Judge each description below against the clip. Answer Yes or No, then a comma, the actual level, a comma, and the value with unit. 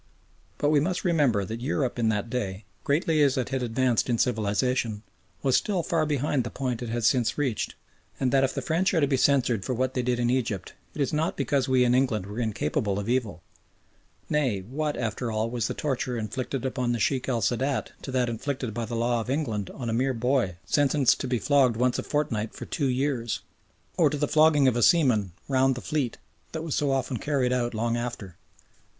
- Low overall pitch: Yes, low, 125 Hz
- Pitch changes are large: No, average, 3.3 semitones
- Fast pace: Yes, fast, 215 wpm